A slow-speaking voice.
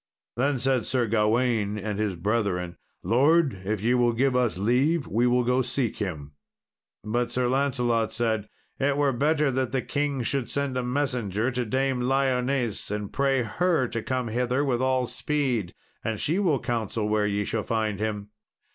No: average, 175 wpm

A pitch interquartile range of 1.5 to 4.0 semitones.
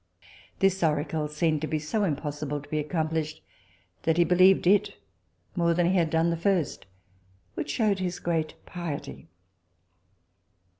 Yes: average, 2.9 semitones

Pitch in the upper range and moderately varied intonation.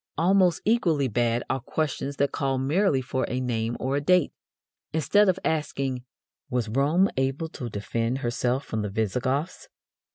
No: low, 135 Hz; average, 4.6 semitones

